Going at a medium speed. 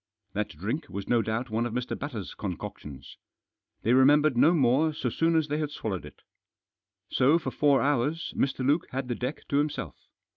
Yes: average, 180 wpm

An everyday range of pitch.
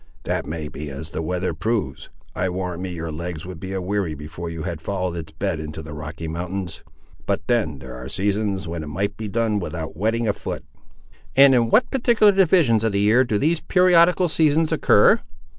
No: wide, 6.2 semitones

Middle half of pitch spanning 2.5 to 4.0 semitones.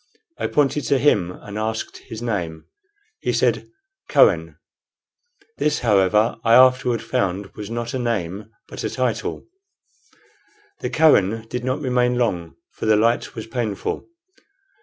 Yes: average, 3.3 semitones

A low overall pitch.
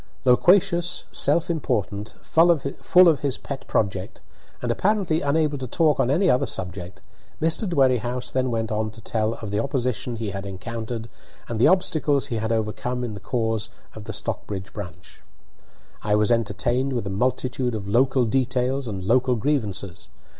Yes: low, 120 Hz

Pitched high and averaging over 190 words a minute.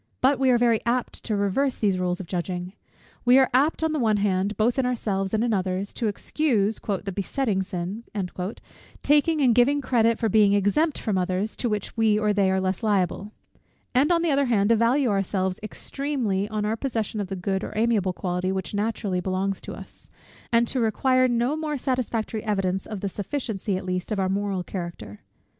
Yes: high, 210 Hz; average, 200 wpm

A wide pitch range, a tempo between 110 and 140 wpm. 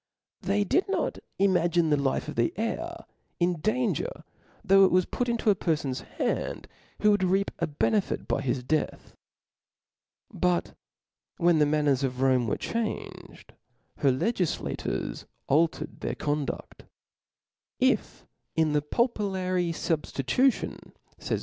Yes: wide, 5.7 semitones; slow, 135 wpm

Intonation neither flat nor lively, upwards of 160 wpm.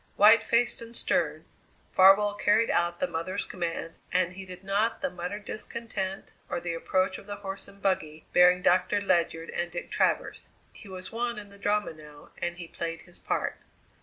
Yes: average, 3.0 semitones; average, 180 wpm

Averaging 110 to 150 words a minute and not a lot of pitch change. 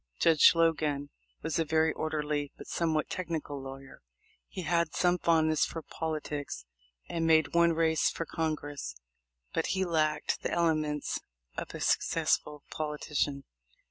Yes: average, 140 wpm; narrow, 1.9 semitones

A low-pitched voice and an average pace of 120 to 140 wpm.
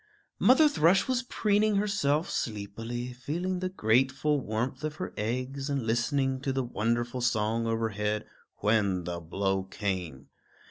Yes: low, 120 Hz; slow, 135 wpm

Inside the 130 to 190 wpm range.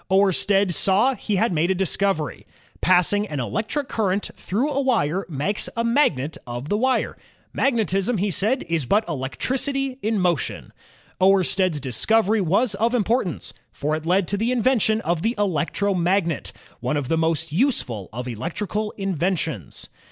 Yes: average, 150 wpm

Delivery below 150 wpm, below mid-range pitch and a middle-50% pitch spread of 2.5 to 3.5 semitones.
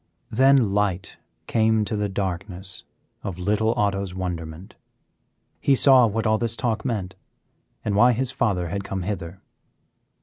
Yes: average, 140 wpm; low, 105 Hz; average, 3.1 semitones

